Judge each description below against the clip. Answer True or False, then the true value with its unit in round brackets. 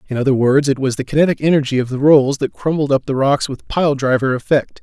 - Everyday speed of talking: False (250 wpm)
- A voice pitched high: False (140 Hz)